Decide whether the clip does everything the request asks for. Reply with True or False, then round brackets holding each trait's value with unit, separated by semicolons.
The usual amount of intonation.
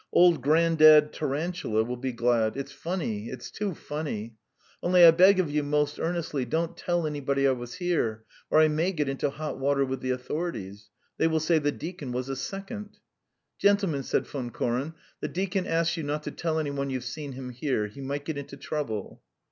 True (4.2 semitones)